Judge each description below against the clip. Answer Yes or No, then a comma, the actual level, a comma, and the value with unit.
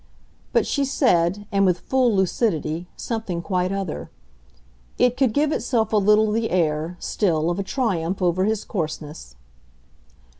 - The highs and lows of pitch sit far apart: No, average, 4.6 semitones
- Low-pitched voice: No, high, 195 Hz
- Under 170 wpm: Yes, average, 145 wpm